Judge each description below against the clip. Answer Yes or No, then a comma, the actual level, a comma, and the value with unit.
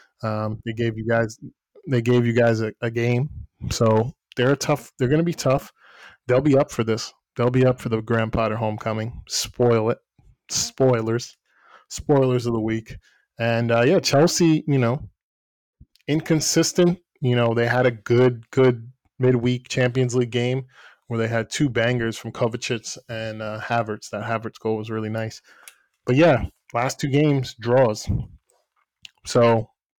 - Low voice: Yes, low, 120 Hz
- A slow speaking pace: No, average, 165 wpm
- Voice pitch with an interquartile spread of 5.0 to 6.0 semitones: No, narrow, 2.4 semitones